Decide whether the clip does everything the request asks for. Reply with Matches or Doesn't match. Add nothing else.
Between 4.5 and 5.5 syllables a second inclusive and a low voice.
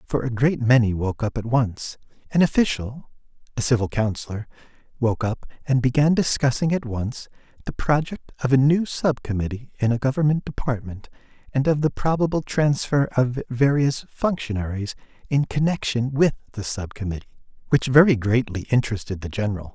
Matches